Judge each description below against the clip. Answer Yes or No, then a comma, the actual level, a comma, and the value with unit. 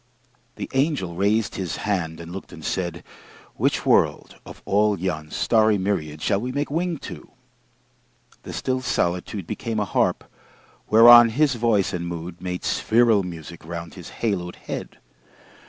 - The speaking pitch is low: Yes, low, 100 Hz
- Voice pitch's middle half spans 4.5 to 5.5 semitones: Yes, average, 5.0 semitones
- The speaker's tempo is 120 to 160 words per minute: Yes, average, 150 wpm